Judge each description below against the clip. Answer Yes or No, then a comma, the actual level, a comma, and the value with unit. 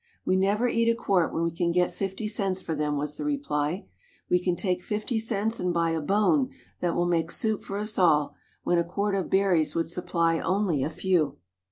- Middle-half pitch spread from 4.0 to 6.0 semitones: No, average, 3.6 semitones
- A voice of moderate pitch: Yes, medium, 180 Hz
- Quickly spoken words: Yes, fast, 215 wpm